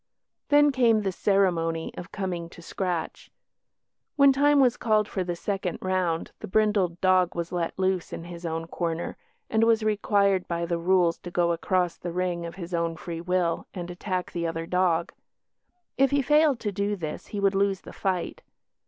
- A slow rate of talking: No, average, 185 wpm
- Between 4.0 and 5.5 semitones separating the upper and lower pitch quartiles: No, average, 3.1 semitones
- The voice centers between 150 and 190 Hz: Yes, medium, 185 Hz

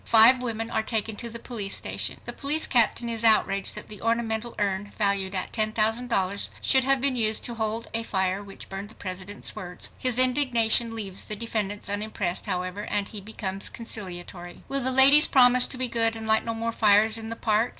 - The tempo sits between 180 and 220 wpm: Yes, average, 200 wpm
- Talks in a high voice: Yes, high, 220 Hz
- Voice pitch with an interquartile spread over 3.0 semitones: No, average, 2.7 semitones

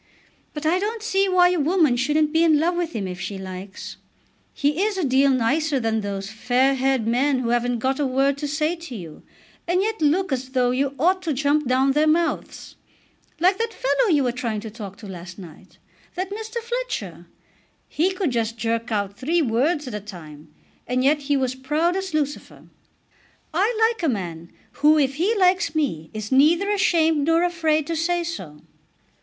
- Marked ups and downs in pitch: Yes, wide, 6.5 semitones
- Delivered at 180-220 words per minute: Yes, average, 195 wpm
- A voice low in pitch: No, very high, 285 Hz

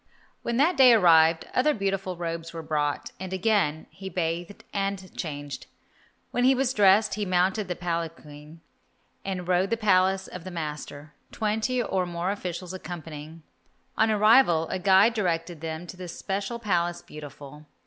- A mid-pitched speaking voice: Yes, medium, 180 Hz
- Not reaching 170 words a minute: Yes, average, 160 wpm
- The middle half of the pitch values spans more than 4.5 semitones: No, average, 3.7 semitones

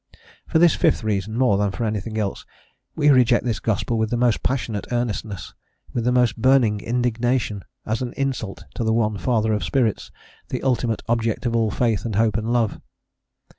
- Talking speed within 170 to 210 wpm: Yes, average, 195 wpm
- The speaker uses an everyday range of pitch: No, narrow, 2.2 semitones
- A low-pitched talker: Yes, low, 115 Hz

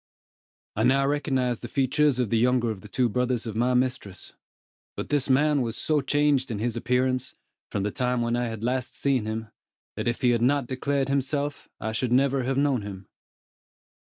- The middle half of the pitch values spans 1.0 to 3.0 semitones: Yes, average, 2.7 semitones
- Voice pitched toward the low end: Yes, low, 125 Hz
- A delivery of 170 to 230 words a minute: Yes, average, 195 wpm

